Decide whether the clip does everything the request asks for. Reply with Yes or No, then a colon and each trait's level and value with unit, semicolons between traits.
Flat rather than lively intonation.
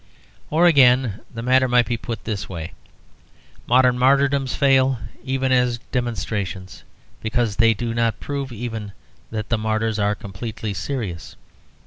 No: average, 3.3 semitones